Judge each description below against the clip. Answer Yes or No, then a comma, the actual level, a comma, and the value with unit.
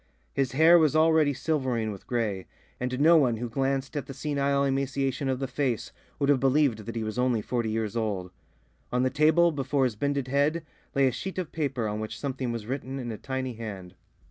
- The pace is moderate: No, fast, 210 wpm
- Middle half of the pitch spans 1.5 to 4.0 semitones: Yes, average, 3.3 semitones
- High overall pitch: No, low, 130 Hz